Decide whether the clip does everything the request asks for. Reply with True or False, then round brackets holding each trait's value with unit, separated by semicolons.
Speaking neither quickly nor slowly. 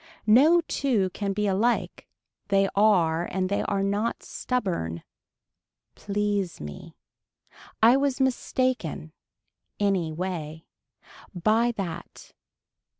False (95 wpm)